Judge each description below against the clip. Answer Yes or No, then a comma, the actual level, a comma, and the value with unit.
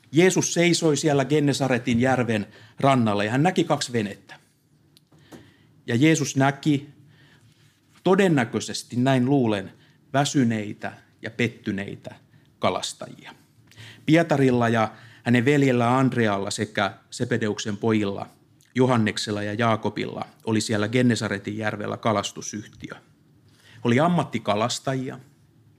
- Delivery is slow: Yes, slow, 90 wpm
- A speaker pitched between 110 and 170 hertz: Yes, low, 120 Hz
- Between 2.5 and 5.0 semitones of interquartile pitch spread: Yes, average, 4.4 semitones